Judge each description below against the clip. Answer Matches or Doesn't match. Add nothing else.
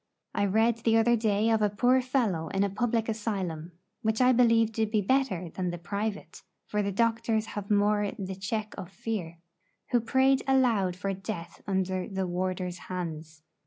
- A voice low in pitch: Doesn't match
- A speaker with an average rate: Matches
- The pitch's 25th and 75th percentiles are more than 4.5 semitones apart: Doesn't match